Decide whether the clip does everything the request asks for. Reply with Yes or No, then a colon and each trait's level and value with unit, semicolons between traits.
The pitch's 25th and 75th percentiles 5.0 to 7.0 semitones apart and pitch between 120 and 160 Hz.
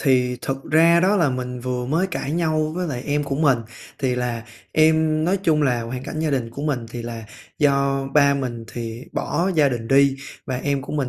No: average, 3.8 semitones; medium, 140 Hz